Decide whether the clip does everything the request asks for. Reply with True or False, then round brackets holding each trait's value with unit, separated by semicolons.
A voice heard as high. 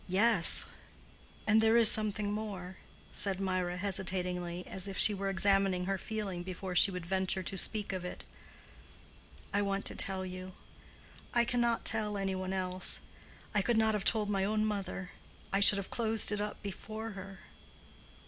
True (195 Hz)